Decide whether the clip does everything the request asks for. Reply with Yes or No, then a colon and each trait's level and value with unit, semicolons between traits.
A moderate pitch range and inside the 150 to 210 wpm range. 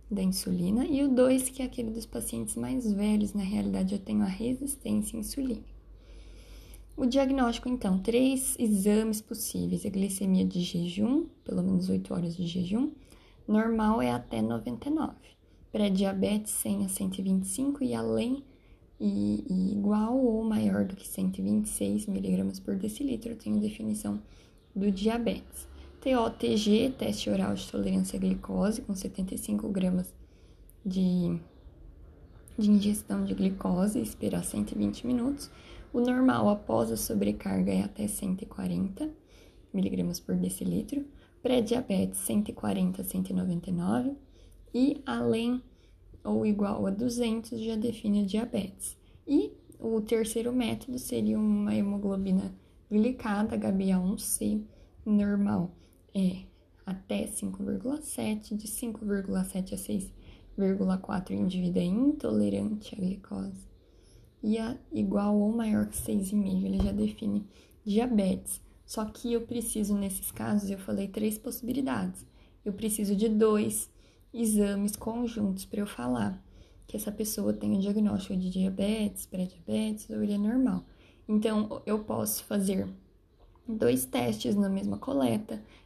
No: average, 4.7 semitones; average, 125 wpm